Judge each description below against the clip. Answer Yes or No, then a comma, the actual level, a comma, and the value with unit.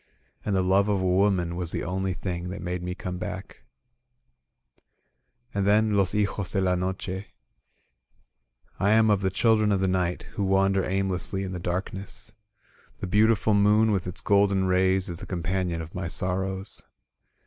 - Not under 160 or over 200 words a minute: Yes, average, 170 wpm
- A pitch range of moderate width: No, narrow, 1.8 semitones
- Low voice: Yes, very low, 95 Hz